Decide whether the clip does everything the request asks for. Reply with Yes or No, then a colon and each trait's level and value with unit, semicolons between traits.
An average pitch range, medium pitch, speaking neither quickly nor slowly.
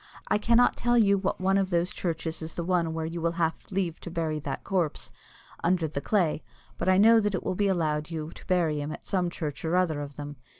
No: average, 3.1 semitones; medium, 170 Hz; fast, 245 wpm